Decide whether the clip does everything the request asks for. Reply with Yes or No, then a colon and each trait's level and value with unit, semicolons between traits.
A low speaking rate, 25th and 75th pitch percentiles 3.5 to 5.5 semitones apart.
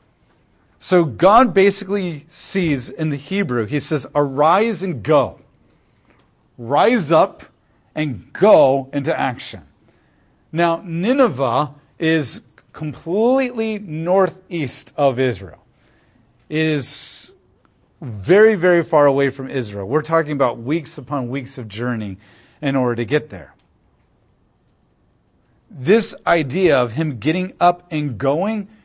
Yes: slow, 110 wpm; average, 5.1 semitones